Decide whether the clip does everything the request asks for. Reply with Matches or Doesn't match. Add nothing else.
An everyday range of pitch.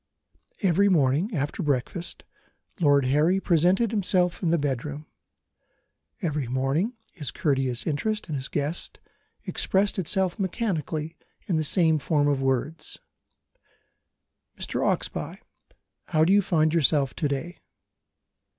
Matches